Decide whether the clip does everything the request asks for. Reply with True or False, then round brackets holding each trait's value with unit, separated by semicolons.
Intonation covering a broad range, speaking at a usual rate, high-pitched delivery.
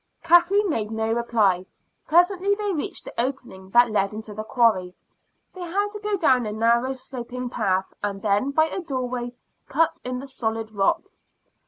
True (6.8 semitones; 170 wpm; 245 Hz)